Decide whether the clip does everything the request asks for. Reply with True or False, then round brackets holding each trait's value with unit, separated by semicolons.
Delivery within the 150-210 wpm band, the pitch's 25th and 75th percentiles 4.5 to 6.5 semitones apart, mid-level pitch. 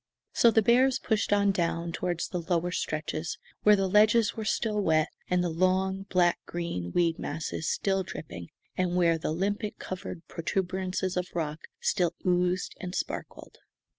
False (160 wpm; 2.7 semitones; 180 Hz)